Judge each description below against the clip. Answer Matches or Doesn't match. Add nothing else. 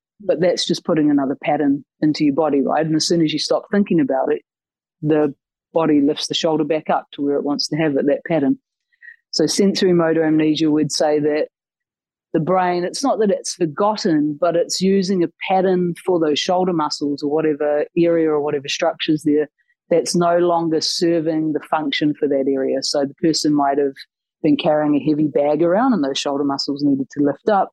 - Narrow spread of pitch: Doesn't match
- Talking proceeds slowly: Doesn't match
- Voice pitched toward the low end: Doesn't match